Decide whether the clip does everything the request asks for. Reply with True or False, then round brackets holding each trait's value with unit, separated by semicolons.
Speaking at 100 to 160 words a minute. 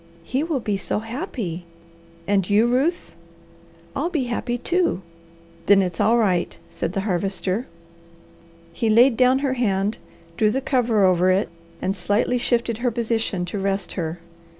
True (150 wpm)